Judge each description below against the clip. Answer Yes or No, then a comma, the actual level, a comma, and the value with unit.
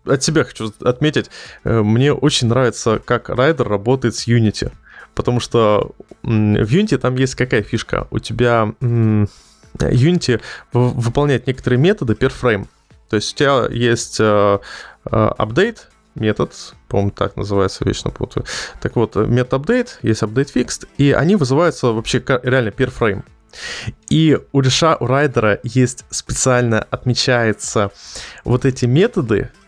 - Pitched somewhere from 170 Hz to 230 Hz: No, low, 120 Hz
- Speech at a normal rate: Yes, average, 130 wpm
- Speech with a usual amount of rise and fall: Yes, average, 3.2 semitones